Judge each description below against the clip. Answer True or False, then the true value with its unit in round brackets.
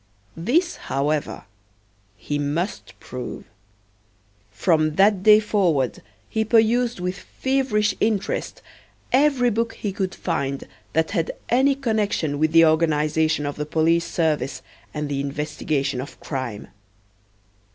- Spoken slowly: True (120 wpm)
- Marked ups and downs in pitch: True (6.5 semitones)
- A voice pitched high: False (165 Hz)